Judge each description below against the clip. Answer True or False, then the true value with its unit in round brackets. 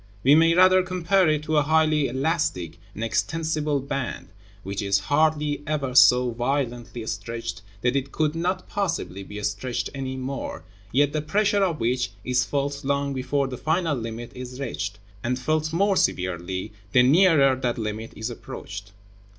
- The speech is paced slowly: False (160 wpm)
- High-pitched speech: False (135 Hz)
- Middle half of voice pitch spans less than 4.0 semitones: False (4.8 semitones)